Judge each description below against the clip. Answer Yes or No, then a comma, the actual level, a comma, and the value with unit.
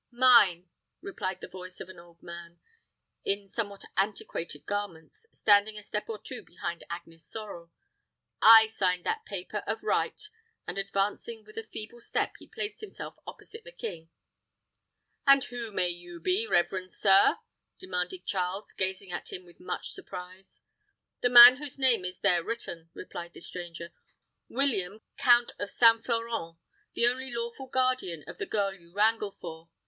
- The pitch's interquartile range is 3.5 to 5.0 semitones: Yes, average, 4.7 semitones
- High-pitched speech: Yes, high, 200 Hz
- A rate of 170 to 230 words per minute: No, average, 155 wpm